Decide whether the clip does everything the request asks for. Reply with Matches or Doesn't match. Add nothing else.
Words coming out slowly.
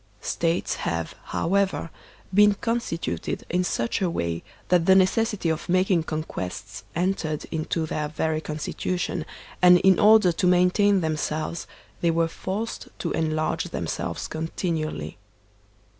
Matches